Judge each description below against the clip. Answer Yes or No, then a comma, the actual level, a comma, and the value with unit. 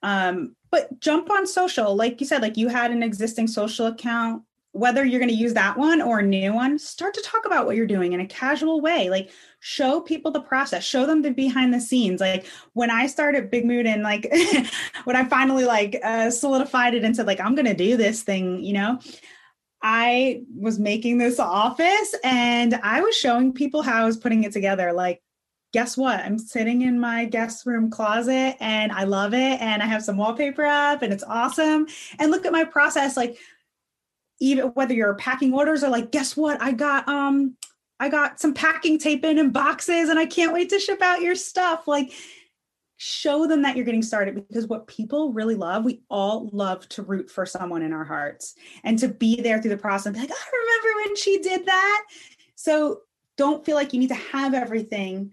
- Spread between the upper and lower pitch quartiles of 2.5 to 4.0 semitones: No, average, 5.1 semitones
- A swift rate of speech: Yes, fast, 210 wpm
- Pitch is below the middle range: No, very high, 250 Hz